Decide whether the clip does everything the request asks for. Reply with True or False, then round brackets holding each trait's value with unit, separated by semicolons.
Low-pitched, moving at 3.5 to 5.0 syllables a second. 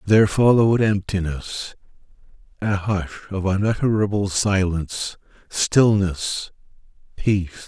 True (100 Hz; 4.3 syllables/s)